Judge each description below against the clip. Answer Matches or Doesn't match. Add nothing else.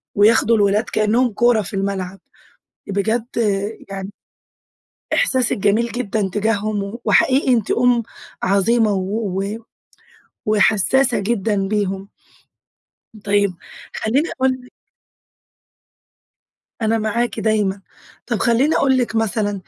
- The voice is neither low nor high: Doesn't match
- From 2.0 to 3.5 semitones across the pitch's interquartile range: Matches